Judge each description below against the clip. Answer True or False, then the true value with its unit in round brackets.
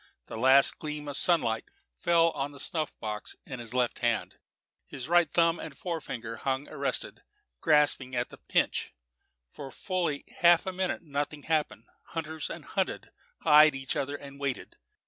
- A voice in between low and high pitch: True (145 Hz)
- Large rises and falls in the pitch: False (3.6 semitones)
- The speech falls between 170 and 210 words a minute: False (160 wpm)